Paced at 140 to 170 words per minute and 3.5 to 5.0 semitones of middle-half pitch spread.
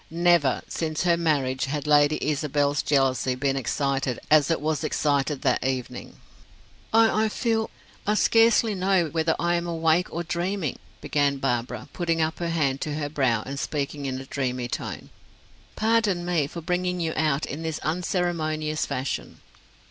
Yes: average, 160 wpm; average, 3.9 semitones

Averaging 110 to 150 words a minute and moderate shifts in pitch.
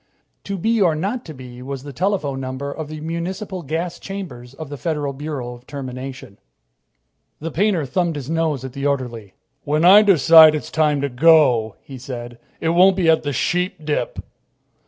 No: average, 180 wpm; average, 4.2 semitones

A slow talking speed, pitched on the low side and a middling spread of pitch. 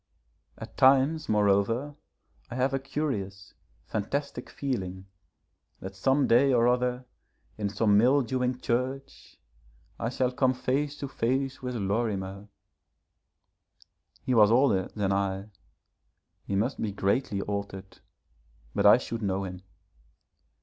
Yes: slow, 120 wpm; low, 120 Hz; average, 4.9 semitones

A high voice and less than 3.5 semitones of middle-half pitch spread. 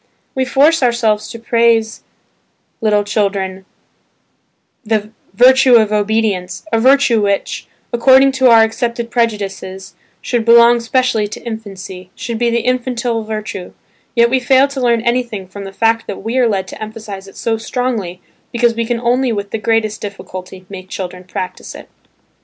Yes: high, 225 Hz; average, 3.0 semitones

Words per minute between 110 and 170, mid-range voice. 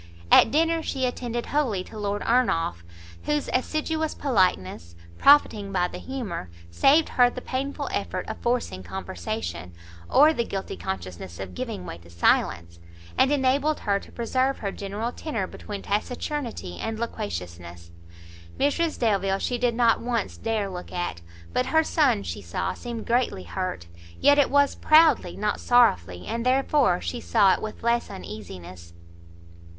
No: average, 150 wpm; high, 215 Hz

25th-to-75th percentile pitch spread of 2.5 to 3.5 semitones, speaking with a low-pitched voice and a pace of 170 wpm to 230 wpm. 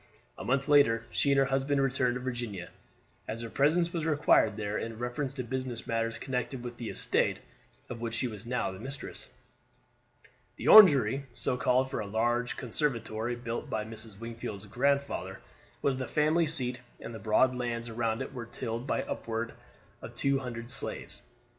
Yes: average, 2.9 semitones; low, 120 Hz; average, 175 wpm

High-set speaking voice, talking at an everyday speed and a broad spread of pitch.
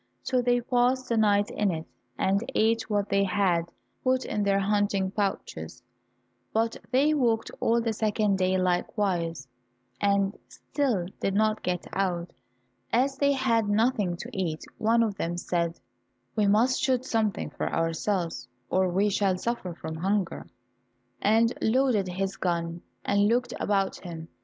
No: high, 205 Hz; average, 150 wpm; average, 3.8 semitones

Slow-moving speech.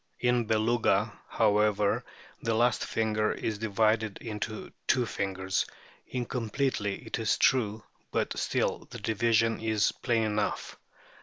Yes: slow, 120 wpm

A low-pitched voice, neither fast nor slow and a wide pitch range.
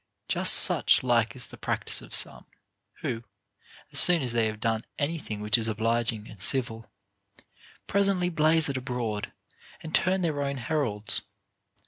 Yes: low, 120 Hz; average, 155 wpm; wide, 5.8 semitones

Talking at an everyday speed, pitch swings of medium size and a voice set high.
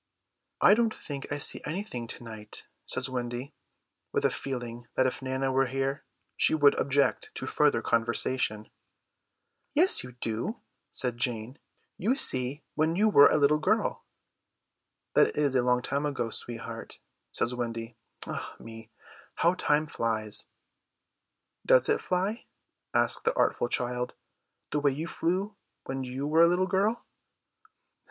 No: average, 145 wpm; average, 4.6 semitones; low, 135 Hz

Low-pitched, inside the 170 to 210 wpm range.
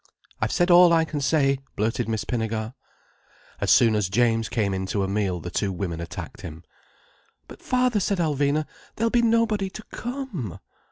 Yes: low, 125 Hz; average, 175 wpm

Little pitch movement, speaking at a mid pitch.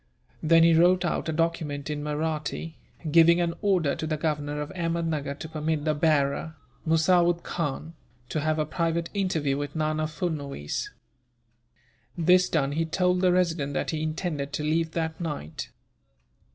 Yes: narrow, 2.1 semitones; medium, 160 Hz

